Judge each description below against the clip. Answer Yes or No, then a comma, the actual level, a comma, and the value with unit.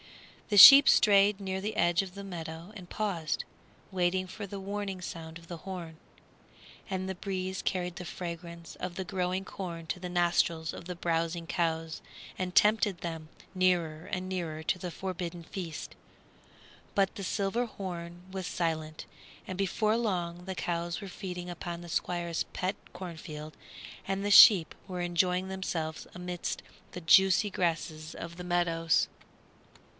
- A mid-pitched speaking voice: Yes, medium, 180 Hz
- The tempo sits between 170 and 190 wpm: No, average, 155 wpm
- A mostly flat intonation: Yes, narrow, 2.1 semitones